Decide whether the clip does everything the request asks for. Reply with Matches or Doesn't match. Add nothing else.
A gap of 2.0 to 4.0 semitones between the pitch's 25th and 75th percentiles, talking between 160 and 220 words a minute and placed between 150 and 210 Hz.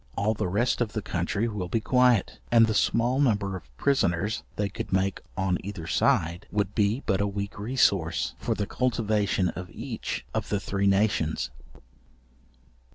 Doesn't match